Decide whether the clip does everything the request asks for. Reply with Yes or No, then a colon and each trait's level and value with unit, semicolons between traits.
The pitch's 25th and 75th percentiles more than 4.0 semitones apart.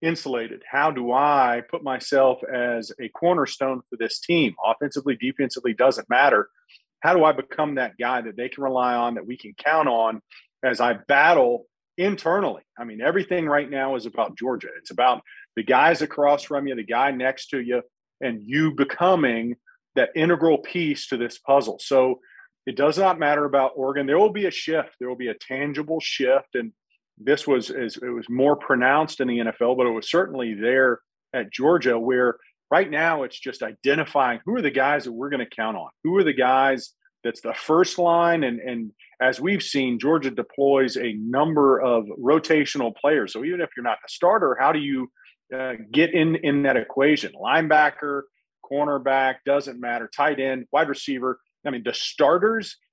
No: average, 3.5 semitones